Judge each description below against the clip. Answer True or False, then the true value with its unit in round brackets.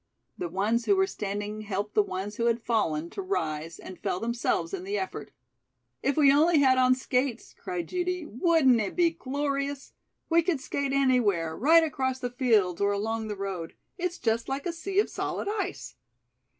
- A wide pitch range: True (7.7 semitones)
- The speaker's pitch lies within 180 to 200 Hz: False (255 Hz)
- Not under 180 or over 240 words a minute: True (185 wpm)